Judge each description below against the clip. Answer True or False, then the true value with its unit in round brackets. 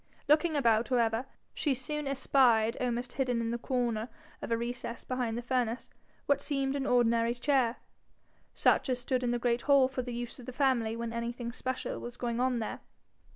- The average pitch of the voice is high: True (245 Hz)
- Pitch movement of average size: False (1.9 semitones)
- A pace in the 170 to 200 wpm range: True (190 wpm)